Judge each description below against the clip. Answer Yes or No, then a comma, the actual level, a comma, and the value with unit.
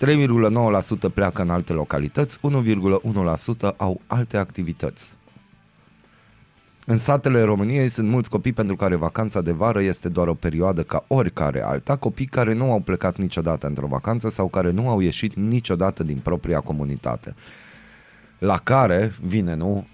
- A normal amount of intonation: Yes, average, 4.8 semitones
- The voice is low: Yes, low, 100 Hz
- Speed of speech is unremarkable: Yes, average, 145 wpm